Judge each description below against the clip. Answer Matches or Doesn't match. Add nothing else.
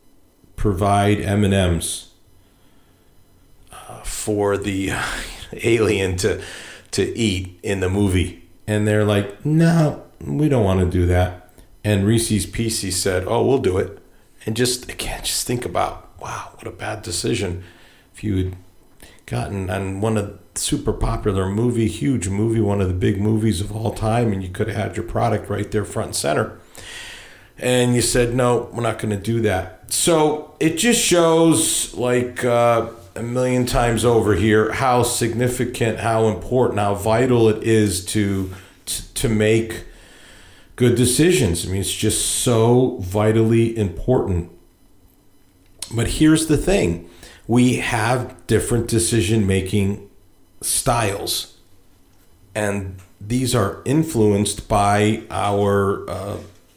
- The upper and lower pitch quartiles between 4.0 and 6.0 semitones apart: Doesn't match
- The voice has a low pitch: Matches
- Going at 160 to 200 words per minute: Doesn't match